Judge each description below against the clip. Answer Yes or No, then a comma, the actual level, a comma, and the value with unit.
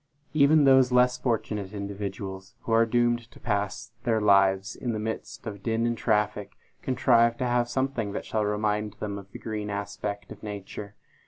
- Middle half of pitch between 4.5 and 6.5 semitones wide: No, average, 2.8 semitones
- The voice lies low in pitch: Yes, low, 105 Hz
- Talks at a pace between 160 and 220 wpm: Yes, average, 175 wpm